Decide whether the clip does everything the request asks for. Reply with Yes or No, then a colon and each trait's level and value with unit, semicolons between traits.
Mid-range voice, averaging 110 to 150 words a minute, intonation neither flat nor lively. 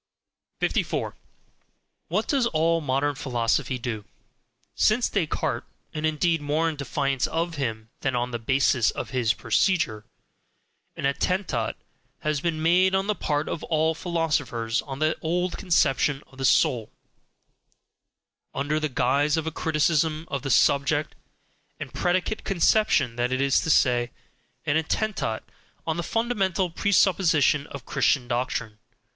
Yes: medium, 150 Hz; average, 140 wpm; average, 4.4 semitones